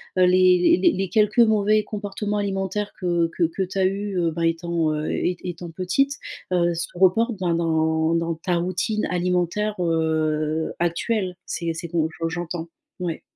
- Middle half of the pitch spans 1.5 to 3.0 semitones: Yes, average, 2.7 semitones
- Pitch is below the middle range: No, medium, 175 Hz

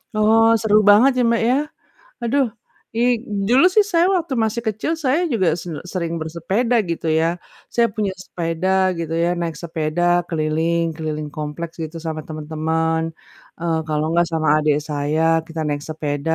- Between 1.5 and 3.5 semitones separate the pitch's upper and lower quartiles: No, wide, 5.5 semitones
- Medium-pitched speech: Yes, medium, 165 Hz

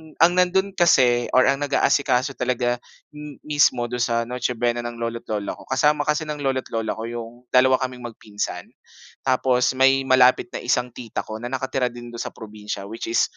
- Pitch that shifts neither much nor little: No, narrow, 2.3 semitones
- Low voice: Yes, low, 125 Hz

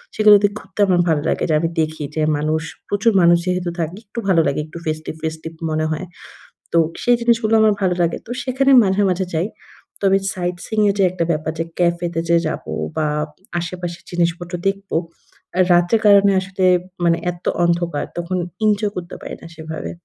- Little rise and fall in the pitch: No, average, 3.1 semitones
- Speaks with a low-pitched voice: No, medium, 175 Hz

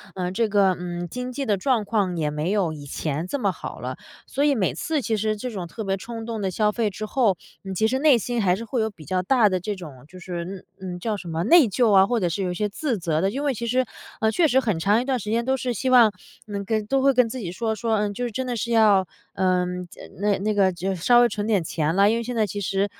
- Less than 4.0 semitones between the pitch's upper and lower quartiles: No, average, 4.3 semitones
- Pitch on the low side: No, high, 210 Hz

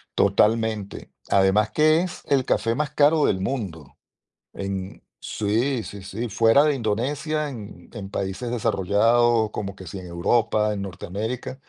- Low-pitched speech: Yes, low, 110 Hz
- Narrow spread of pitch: No, average, 4.4 semitones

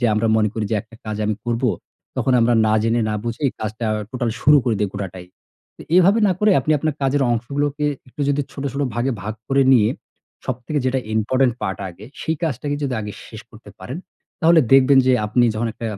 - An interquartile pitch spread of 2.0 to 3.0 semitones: No, average, 4.3 semitones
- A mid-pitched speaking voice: No, low, 120 Hz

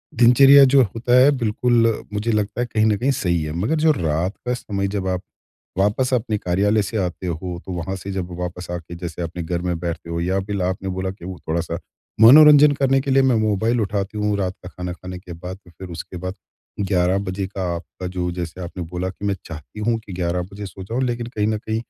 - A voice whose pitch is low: Yes, very low, 95 Hz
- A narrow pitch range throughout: No, average, 3.8 semitones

